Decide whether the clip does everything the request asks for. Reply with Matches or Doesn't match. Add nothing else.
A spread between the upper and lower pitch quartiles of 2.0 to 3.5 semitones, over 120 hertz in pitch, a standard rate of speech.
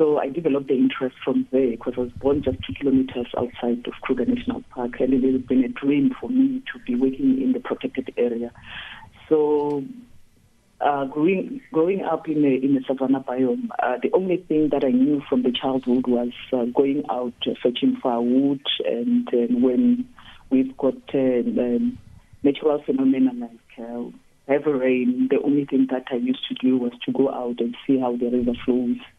Matches